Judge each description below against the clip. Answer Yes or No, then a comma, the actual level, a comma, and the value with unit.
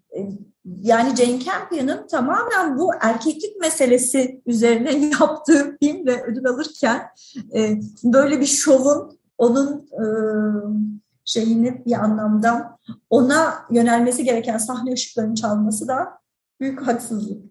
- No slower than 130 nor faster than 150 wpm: No, average, 100 wpm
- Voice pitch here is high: Yes, high, 245 Hz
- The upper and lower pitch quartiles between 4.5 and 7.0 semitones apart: No, average, 4.1 semitones